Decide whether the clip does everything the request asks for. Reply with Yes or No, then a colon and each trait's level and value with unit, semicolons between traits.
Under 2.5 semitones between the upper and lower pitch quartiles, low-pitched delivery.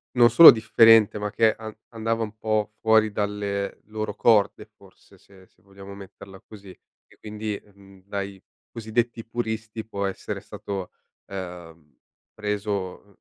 Yes: narrow, 2.0 semitones; low, 105 Hz